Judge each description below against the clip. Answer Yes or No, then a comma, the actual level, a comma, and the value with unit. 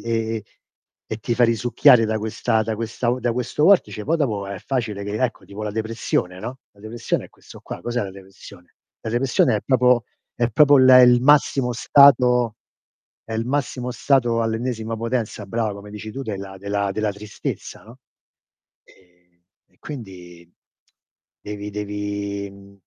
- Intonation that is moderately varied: Yes, average, 3.3 semitones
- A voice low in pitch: Yes, low, 110 Hz